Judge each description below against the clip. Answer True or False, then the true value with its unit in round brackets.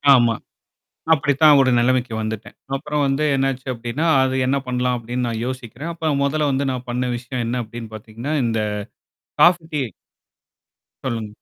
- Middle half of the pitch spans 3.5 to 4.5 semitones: False (3.0 semitones)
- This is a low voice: True (125 Hz)